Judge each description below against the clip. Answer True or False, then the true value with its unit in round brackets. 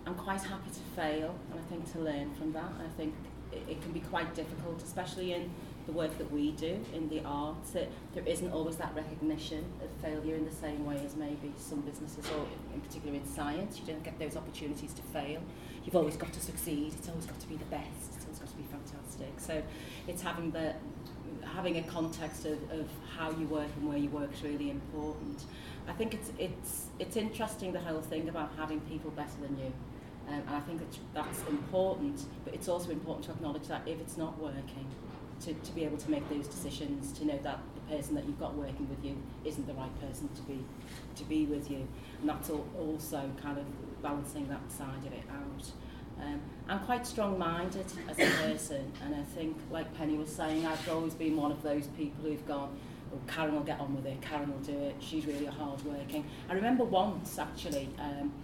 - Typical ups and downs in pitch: False (2.0 semitones)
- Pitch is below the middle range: False (150 Hz)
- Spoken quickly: True (215 wpm)